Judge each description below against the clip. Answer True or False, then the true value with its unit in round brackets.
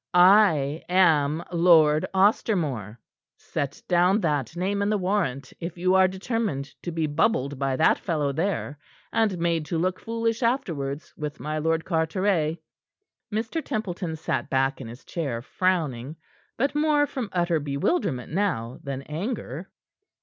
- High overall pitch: False (165 Hz)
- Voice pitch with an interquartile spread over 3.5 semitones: True (5.2 semitones)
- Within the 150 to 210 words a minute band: False (140 wpm)